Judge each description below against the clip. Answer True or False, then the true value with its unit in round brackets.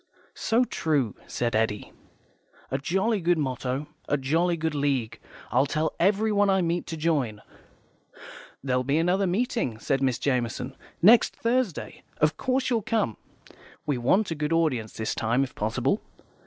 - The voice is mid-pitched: True (155 Hz)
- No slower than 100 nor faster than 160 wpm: True (150 wpm)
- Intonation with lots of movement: True (7.0 semitones)